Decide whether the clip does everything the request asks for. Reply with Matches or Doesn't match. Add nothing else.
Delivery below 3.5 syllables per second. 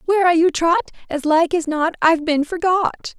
Doesn't match